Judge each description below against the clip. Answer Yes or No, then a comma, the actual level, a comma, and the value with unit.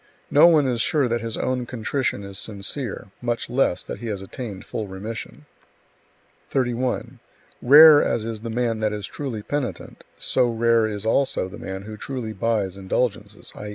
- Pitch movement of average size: Yes, average, 3.2 semitones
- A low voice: Yes, low, 115 Hz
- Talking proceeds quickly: No, average, 170 wpm